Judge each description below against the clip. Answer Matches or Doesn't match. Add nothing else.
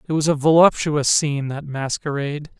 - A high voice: Doesn't match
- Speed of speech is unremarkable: Matches